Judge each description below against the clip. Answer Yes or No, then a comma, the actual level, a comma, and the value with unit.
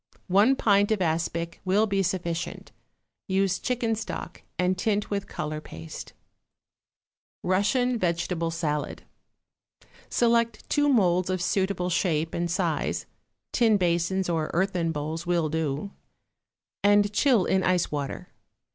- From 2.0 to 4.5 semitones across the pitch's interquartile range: Yes, average, 3.5 semitones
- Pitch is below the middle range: No, medium, 185 Hz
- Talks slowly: Yes, slow, 120 wpm